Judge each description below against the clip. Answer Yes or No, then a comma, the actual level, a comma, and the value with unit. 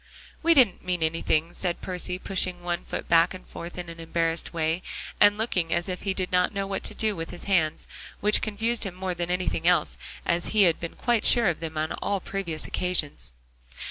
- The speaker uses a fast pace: Yes, fast, 210 wpm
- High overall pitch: No, medium, 180 Hz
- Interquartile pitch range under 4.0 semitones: Yes, average, 2.8 semitones